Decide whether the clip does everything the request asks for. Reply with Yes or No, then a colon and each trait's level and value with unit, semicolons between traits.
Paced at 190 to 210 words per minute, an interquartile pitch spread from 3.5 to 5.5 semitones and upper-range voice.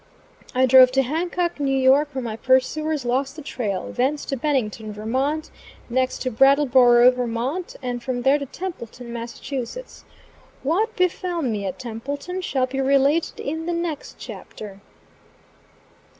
No: slow, 135 wpm; average, 3.8 semitones; very high, 265 Hz